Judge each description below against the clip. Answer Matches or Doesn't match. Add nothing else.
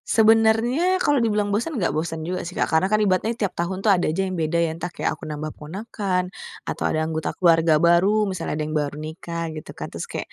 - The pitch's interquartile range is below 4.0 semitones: Doesn't match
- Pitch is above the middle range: Doesn't match